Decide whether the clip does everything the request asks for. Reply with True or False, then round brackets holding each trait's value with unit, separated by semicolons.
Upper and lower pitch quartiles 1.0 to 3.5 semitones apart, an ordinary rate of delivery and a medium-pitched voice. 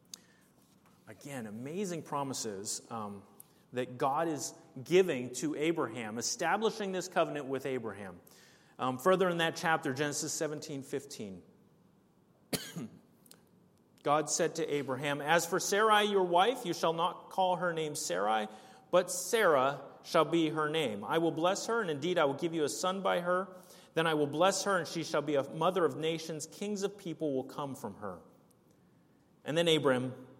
False (4.1 semitones; 160 wpm; 160 Hz)